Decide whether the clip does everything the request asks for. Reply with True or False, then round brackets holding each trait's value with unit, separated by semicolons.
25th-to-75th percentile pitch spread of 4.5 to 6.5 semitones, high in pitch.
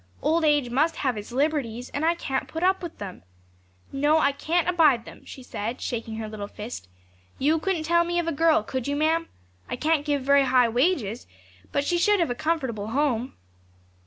True (5.1 semitones; 285 Hz)